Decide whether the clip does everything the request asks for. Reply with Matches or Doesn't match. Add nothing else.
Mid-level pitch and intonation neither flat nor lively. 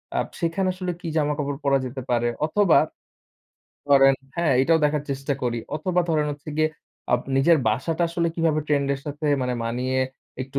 Matches